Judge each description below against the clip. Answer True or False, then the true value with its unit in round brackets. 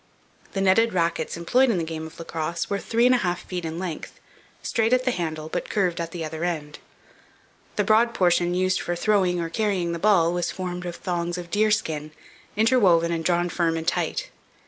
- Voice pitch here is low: False (175 Hz)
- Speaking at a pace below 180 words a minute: False (200 wpm)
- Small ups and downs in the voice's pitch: False (3.5 semitones)